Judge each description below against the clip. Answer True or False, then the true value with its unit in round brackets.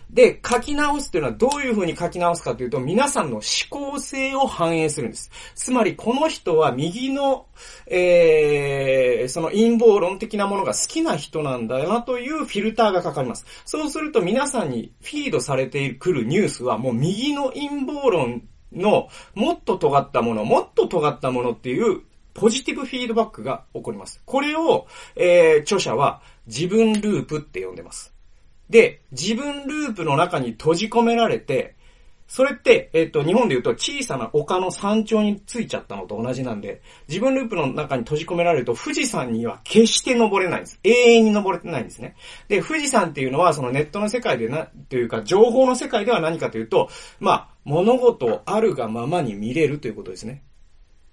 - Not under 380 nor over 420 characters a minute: True (385 characters per minute)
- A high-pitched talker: True (225 Hz)